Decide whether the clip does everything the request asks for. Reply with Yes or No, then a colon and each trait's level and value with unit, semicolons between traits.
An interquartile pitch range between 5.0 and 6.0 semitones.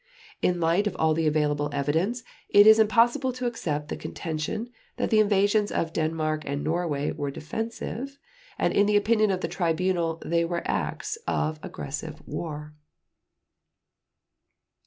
Yes: wide, 5.5 semitones